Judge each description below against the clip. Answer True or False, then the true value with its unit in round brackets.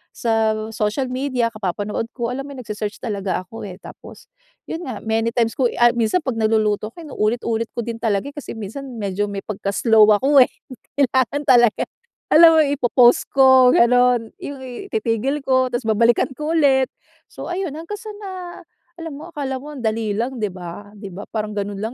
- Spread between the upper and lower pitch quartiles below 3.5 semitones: False (3.8 semitones)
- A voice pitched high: True (235 Hz)